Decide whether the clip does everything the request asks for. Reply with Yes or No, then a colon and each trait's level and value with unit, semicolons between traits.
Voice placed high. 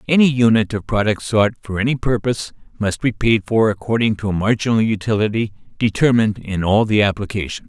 No: low, 110 Hz